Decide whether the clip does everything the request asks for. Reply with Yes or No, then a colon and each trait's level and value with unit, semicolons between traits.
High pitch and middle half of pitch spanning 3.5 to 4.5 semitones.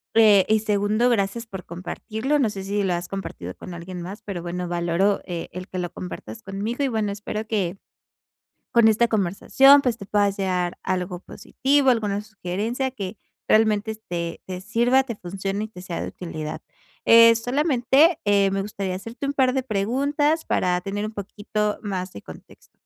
Yes: high, 205 Hz; average, 3.9 semitones